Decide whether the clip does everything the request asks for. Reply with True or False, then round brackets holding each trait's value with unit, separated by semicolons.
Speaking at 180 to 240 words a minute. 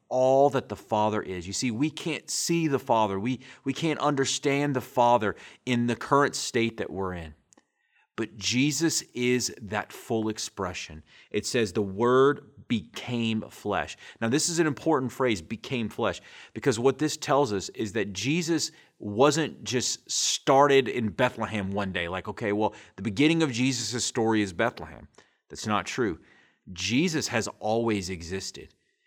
False (160 wpm)